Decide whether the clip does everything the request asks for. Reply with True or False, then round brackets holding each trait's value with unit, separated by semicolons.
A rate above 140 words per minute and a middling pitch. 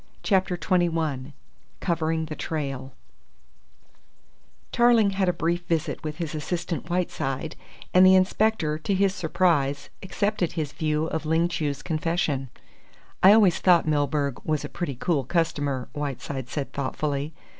False (135 wpm; 160 Hz)